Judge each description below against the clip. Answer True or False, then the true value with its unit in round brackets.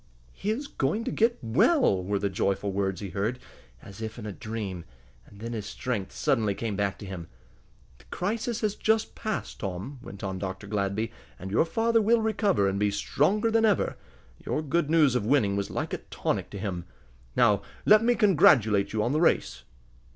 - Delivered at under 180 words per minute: False (195 wpm)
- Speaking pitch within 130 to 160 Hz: False (110 Hz)